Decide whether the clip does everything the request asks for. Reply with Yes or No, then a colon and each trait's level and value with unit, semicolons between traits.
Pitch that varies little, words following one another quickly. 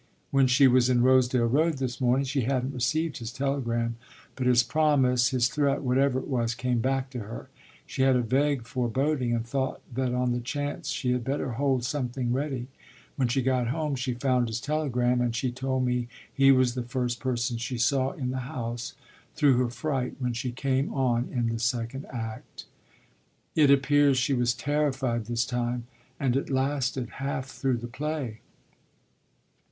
No: narrow, 2.1 semitones; average, 180 wpm